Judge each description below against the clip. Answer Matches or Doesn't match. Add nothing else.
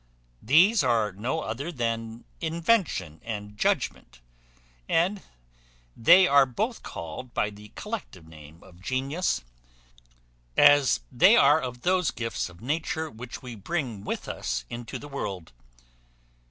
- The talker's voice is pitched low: Matches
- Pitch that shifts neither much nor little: Doesn't match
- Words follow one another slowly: Matches